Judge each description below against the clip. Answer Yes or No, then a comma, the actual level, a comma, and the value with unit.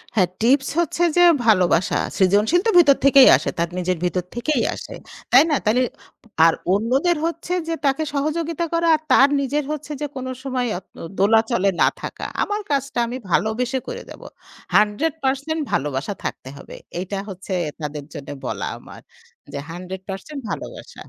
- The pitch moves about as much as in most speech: No, wide, 7.8 semitones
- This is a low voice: No, very high, 250 Hz